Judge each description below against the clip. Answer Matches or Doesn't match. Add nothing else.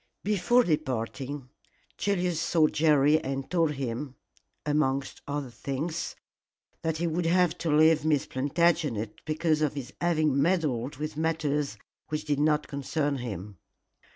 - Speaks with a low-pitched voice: Doesn't match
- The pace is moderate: Doesn't match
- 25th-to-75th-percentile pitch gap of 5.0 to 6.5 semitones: Doesn't match